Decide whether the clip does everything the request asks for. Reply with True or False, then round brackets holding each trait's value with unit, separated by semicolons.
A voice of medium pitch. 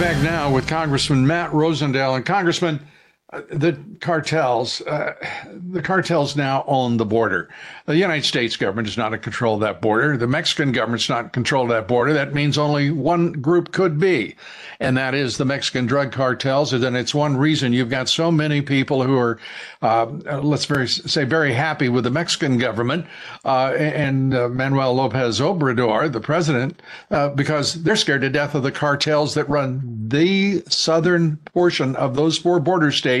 True (145 Hz)